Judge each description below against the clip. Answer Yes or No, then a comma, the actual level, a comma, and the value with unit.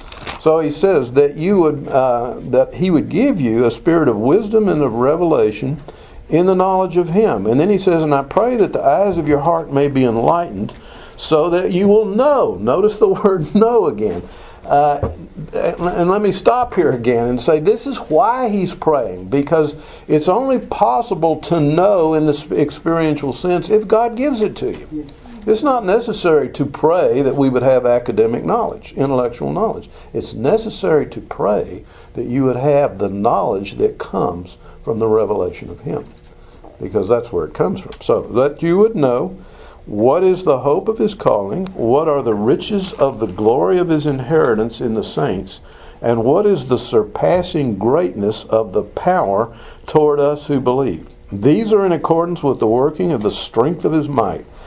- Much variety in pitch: Yes, wide, 6.9 semitones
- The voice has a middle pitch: Yes, medium, 160 Hz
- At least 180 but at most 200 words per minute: Yes, average, 185 wpm